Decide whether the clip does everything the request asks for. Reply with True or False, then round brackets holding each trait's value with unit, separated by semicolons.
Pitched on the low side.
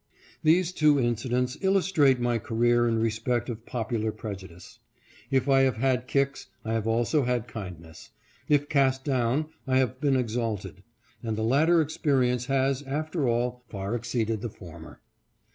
True (125 Hz)